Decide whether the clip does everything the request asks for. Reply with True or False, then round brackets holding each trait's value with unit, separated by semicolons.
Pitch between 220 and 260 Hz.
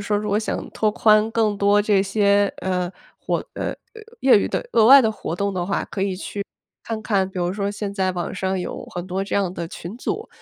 False (200 Hz)